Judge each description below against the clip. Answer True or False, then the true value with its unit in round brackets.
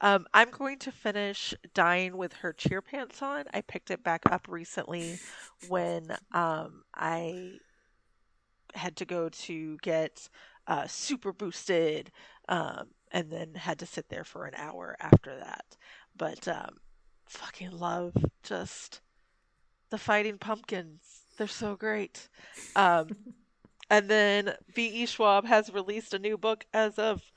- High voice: True (195 Hz)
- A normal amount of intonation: True (4.1 semitones)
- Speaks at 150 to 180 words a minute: False (140 wpm)